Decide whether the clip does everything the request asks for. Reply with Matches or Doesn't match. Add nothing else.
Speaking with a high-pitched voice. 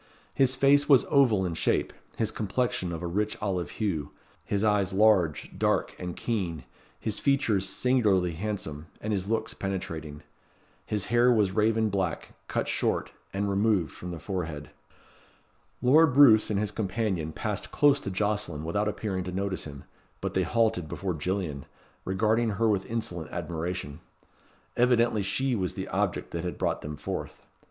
Doesn't match